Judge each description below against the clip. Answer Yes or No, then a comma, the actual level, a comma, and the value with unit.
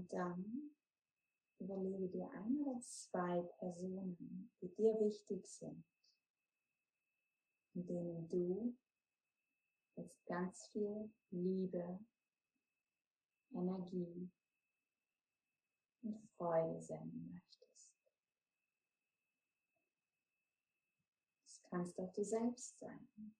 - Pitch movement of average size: Yes, average, 3.5 semitones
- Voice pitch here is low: No, high, 190 Hz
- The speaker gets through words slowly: Yes, slow, 75 wpm